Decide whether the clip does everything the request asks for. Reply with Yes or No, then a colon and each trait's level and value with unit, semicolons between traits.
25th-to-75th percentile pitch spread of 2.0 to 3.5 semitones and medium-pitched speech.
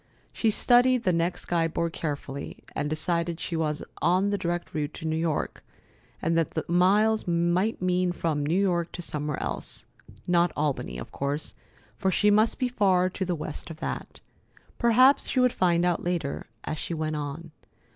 Yes: average, 3.2 semitones; medium, 170 Hz